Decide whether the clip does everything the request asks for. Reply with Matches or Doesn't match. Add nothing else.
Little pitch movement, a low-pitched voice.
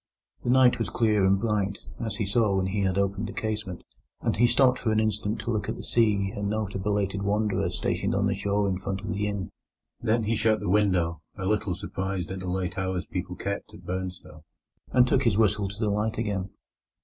Matches